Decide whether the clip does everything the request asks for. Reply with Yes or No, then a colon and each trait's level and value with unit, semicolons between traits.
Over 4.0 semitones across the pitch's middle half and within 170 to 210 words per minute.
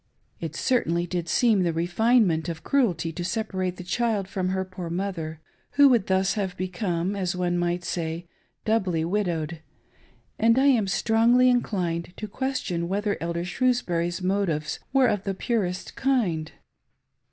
No: average, 4.4 semitones; average, 150 wpm